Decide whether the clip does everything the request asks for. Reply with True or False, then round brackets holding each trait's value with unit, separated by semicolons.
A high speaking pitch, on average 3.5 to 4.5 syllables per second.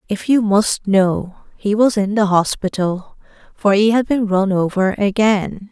True (205 Hz; 4.0 syllables/s)